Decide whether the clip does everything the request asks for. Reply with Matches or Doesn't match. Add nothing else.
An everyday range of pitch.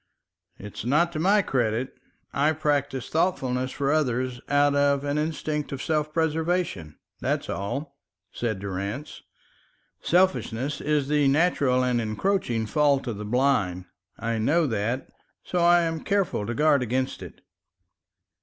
Matches